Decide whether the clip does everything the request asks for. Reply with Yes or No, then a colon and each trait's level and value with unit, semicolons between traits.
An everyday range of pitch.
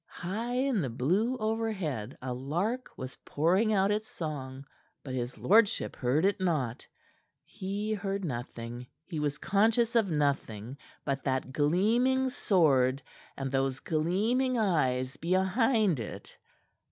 No: wide, 8.3 semitones